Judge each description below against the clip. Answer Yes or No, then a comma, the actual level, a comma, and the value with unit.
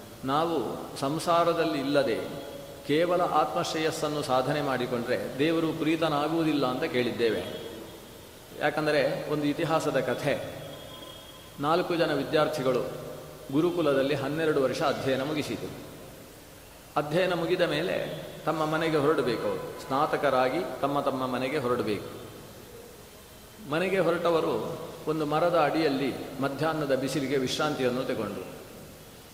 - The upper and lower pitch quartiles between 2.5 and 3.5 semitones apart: Yes, average, 3.1 semitones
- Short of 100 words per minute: Yes, average, 90 wpm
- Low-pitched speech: No, medium, 150 Hz